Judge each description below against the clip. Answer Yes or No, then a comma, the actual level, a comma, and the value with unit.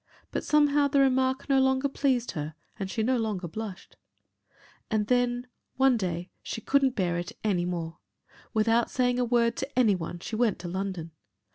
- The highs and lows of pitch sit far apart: Yes, wide, 5.8 semitones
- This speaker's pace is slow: No, average, 175 wpm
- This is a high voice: Yes, high, 230 Hz